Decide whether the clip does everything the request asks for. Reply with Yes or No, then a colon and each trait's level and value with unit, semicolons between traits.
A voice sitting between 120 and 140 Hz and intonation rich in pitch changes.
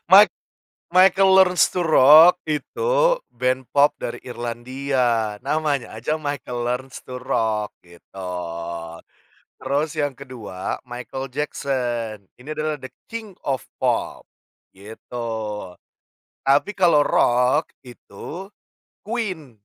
No: low, 135 Hz; average, 4.3 semitones